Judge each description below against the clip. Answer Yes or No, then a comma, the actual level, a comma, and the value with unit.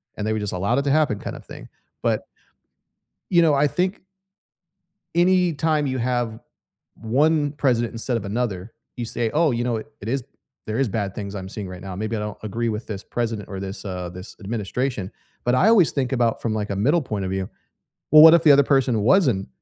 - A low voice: Yes, low, 115 Hz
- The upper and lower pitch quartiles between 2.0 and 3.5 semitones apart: No, wide, 5.4 semitones